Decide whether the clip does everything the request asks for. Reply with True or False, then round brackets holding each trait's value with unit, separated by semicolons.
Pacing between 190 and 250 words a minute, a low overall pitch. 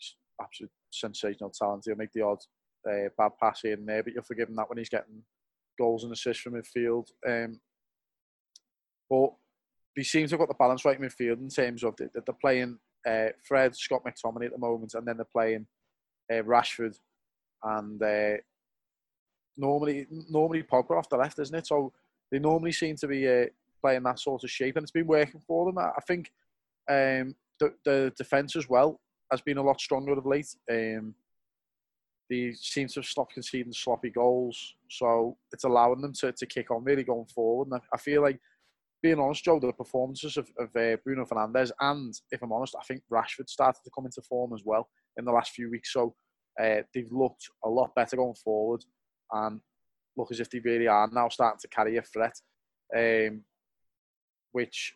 True (195 wpm; 125 Hz)